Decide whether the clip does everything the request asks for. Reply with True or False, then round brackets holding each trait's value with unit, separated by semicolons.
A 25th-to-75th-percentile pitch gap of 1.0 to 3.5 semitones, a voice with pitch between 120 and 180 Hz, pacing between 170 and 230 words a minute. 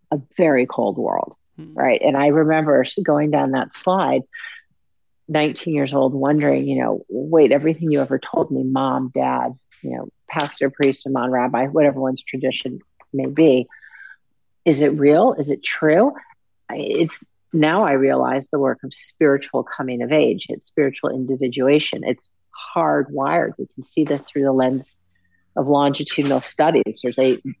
False (2.5 semitones; 140 Hz; 155 wpm)